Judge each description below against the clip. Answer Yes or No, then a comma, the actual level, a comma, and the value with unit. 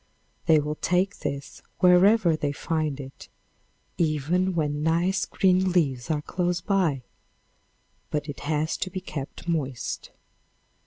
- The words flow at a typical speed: No, slow, 125 wpm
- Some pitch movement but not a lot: Yes, average, 3.6 semitones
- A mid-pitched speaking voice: Yes, medium, 160 Hz